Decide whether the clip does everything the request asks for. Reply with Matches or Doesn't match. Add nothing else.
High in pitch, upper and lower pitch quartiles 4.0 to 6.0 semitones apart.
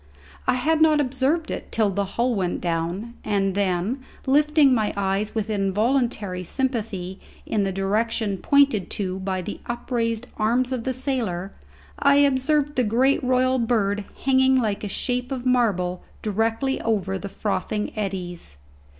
Matches